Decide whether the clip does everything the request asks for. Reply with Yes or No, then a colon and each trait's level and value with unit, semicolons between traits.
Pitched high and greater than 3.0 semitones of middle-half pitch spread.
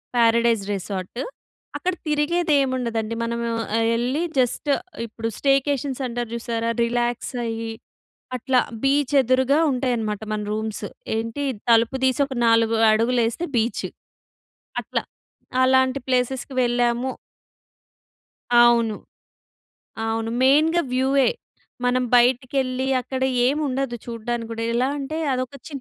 No: high, 245 Hz; narrow, 2.5 semitones